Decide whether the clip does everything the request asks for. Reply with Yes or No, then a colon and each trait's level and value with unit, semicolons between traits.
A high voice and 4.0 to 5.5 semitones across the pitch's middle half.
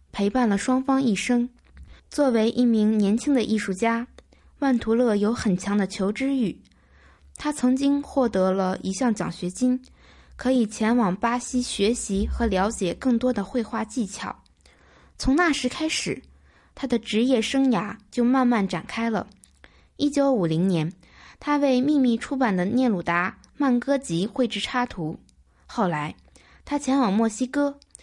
Yes: high, 235 Hz; average, 4.7 semitones